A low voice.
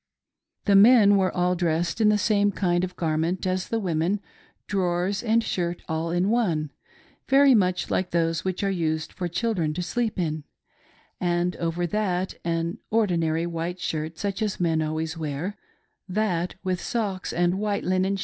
No: medium, 180 Hz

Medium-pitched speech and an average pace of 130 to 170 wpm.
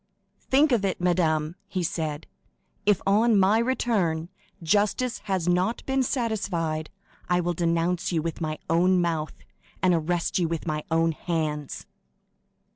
Yes: medium, 175 Hz; average, 140 wpm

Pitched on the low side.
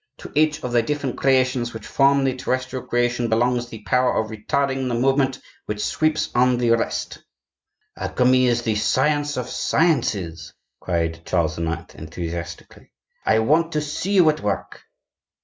Yes: low, 125 Hz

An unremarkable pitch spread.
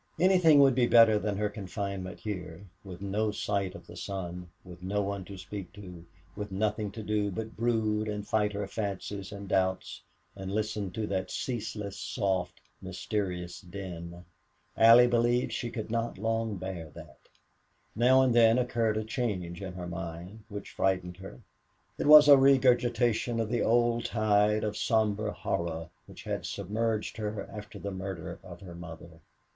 Yes: average, 3.2 semitones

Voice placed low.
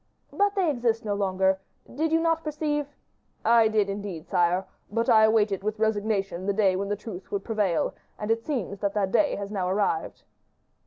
No: high, 210 Hz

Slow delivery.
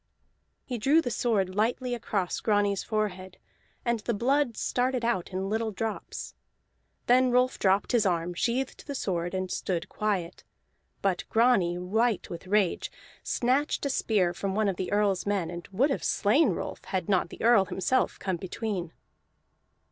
No: average, 160 wpm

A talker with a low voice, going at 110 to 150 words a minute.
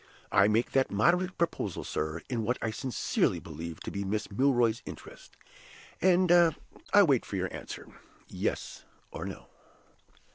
Yes: low, 115 Hz; average, 140 wpm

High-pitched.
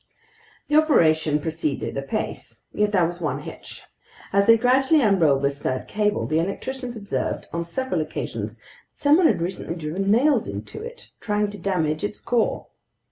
Yes: high, 200 Hz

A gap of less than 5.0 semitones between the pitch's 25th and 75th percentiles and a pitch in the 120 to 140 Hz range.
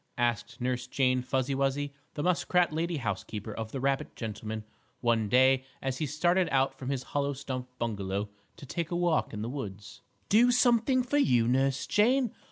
No: average, 5.3 semitones; low, 135 Hz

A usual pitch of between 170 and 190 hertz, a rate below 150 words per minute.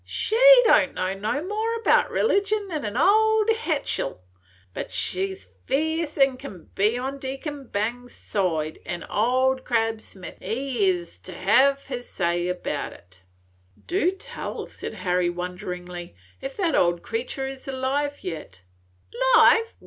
No: very high, 255 Hz; average, 140 wpm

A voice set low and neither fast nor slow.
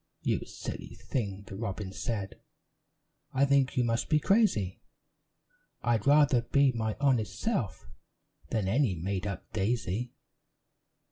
No: low, 115 Hz; slow, 125 wpm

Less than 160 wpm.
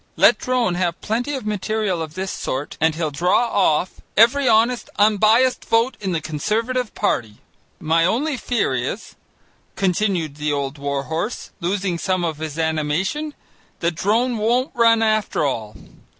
Yes: average, 150 wpm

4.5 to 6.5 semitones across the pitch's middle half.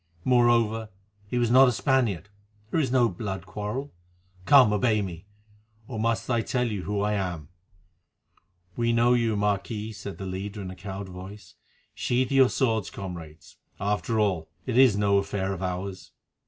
No: average, 3.7 semitones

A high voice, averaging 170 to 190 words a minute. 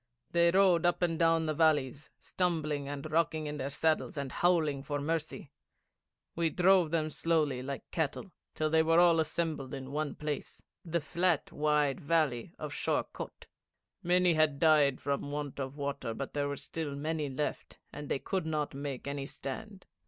No: medium, 155 Hz; average, 175 wpm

